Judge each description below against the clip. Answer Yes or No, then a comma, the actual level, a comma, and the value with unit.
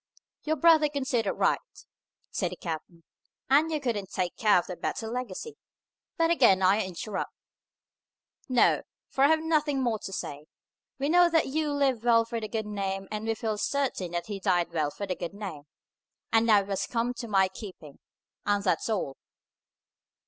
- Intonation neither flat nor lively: No, wide, 6.1 semitones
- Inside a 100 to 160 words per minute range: No, average, 180 wpm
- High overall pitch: Yes, high, 220 Hz